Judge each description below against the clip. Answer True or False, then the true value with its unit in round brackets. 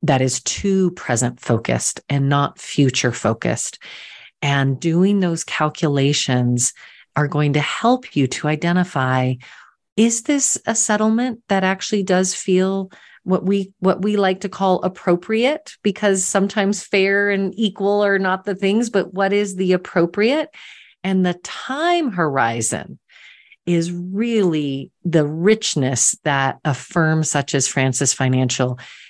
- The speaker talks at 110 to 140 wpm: True (135 wpm)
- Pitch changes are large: True (6.1 semitones)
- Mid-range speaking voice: True (180 Hz)